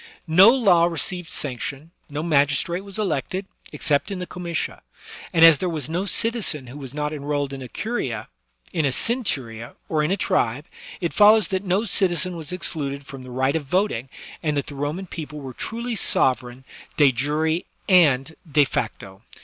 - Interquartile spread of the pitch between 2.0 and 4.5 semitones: No, average, 4.9 semitones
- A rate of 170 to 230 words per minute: Yes, average, 180 wpm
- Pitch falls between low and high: Yes, medium, 155 Hz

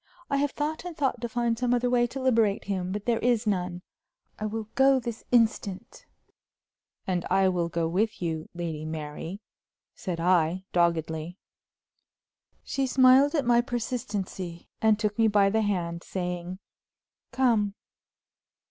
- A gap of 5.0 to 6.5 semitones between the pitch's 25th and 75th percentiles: Yes, wide, 5.4 semitones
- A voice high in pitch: Yes, high, 210 Hz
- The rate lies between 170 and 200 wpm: No, average, 150 wpm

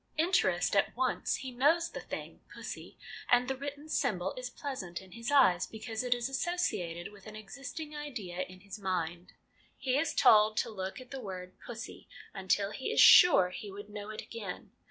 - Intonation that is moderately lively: No, wide, 6.0 semitones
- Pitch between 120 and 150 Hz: No, high, 220 Hz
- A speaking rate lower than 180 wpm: No, average, 195 wpm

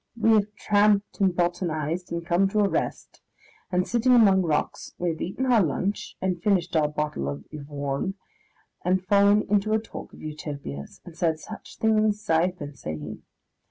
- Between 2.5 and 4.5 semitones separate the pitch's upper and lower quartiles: No, average, 4.9 semitones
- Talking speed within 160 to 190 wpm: Yes, average, 180 wpm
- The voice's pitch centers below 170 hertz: No, medium, 180 Hz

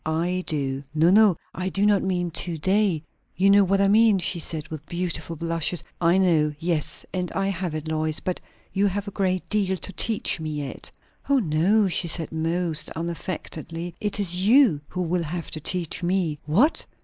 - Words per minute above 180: Yes, average, 190 wpm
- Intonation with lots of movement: No, average, 3.3 semitones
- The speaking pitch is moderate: Yes, medium, 175 Hz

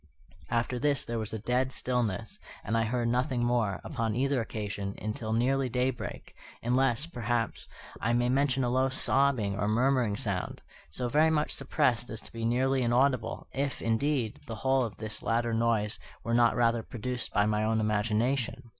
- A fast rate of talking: No, average, 170 wpm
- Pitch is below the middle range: Yes, low, 120 Hz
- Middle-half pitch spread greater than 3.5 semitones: No, average, 2.7 semitones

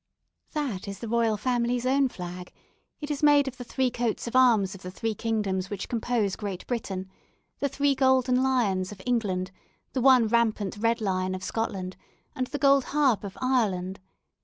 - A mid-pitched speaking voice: No, high, 230 Hz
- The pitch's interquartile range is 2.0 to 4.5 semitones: No, average, 4.9 semitones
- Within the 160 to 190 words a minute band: Yes, average, 180 wpm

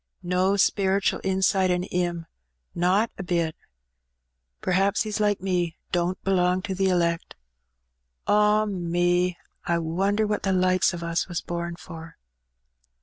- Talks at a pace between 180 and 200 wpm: No, average, 140 wpm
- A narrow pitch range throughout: Yes, narrow, 2.0 semitones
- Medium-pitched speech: Yes, medium, 180 Hz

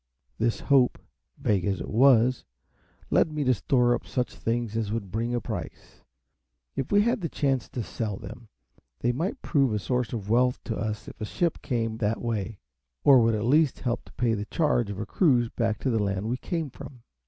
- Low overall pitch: Yes, low, 120 Hz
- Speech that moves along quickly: Yes, fast, 210 wpm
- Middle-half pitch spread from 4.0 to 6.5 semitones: No, average, 3.2 semitones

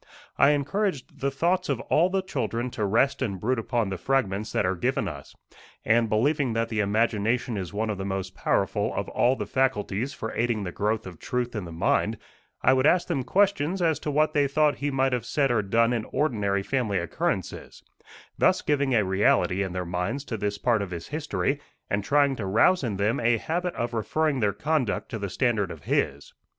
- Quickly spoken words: Yes, fast, 210 wpm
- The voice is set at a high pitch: No, low, 115 Hz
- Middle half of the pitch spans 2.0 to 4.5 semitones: No, wide, 5.5 semitones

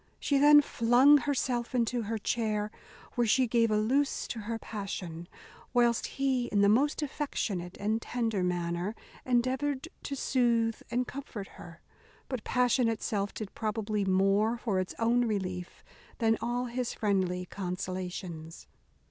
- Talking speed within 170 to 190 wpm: No, average, 140 wpm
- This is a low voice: No, high, 225 Hz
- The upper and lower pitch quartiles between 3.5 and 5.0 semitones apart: Yes, average, 3.9 semitones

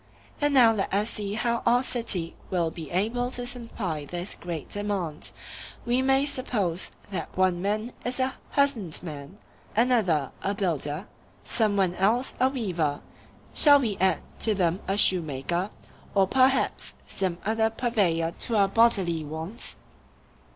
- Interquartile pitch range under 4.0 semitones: No, wide, 5.4 semitones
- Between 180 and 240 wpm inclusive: No, average, 140 wpm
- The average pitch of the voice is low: No, high, 200 Hz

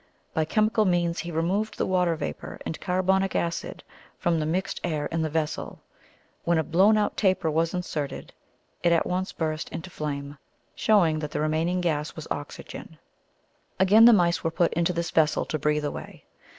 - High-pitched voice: No, medium, 170 Hz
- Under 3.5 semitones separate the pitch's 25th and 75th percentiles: Yes, average, 2.9 semitones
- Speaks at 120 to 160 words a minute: No, average, 175 wpm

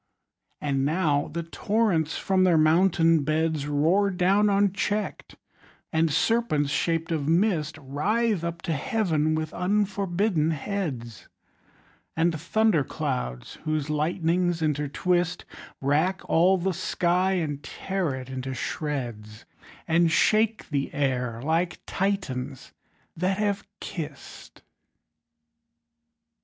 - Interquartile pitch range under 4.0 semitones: No, average, 4.4 semitones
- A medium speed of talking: No, slow, 105 wpm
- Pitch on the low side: No, medium, 165 Hz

